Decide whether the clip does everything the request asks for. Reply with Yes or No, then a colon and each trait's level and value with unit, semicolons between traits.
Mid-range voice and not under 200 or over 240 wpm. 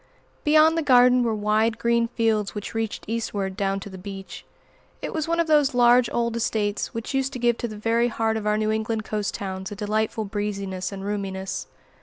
No: high, 220 Hz; fast, 205 wpm